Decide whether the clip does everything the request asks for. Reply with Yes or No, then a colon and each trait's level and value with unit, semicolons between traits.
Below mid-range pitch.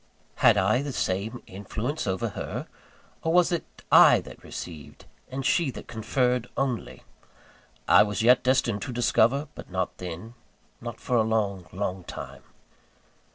Yes: low, 115 Hz